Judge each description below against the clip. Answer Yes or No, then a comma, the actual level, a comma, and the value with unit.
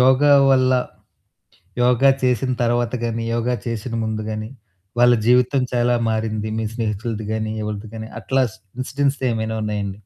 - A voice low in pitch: Yes, low, 115 Hz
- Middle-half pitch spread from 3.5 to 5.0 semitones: No, narrow, 2.5 semitones